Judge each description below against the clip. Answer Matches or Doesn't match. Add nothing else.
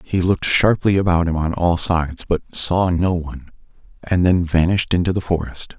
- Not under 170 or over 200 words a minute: Matches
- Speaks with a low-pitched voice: Matches